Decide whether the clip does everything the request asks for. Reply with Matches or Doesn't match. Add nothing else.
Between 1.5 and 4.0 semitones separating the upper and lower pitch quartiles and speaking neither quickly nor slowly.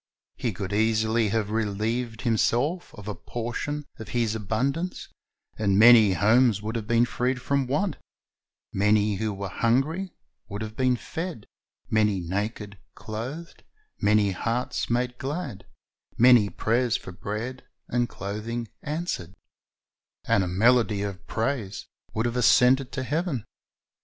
Doesn't match